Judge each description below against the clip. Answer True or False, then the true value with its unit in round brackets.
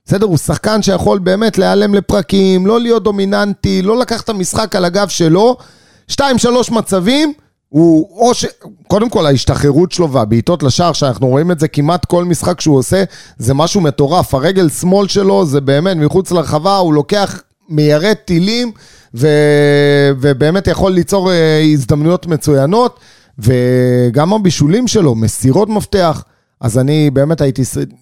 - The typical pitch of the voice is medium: True (175 Hz)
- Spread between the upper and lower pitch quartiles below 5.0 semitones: False (5.6 semitones)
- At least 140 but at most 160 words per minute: True (145 wpm)